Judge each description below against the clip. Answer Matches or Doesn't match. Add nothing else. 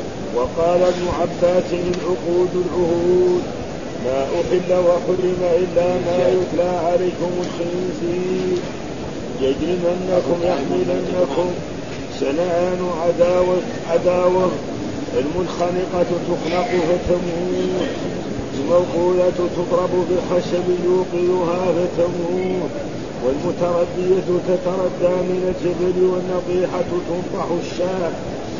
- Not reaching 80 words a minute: Matches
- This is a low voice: Doesn't match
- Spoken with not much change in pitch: Matches